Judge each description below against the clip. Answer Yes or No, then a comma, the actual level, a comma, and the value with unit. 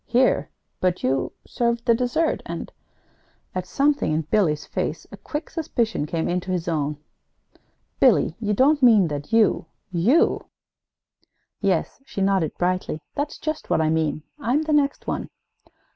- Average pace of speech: Yes, average, 155 wpm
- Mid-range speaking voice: No, high, 195 Hz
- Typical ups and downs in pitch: No, wide, 8.1 semitones